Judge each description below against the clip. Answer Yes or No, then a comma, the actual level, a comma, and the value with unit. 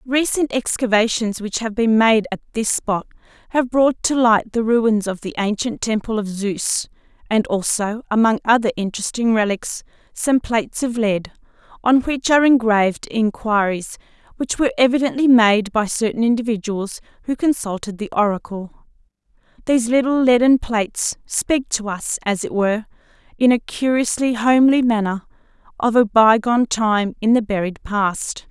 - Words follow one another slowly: No, average, 150 wpm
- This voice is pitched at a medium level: No, high, 225 Hz